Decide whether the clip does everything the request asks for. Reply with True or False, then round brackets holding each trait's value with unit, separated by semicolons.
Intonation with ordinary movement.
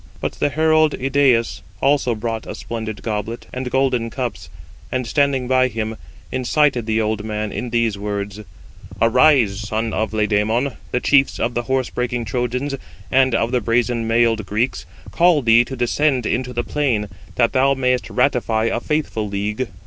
True (3.0 semitones)